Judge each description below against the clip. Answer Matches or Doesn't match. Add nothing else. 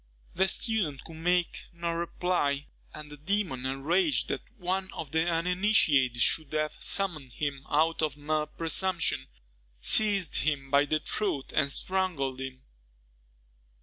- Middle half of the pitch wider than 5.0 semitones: Doesn't match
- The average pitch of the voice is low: Doesn't match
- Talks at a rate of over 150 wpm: Doesn't match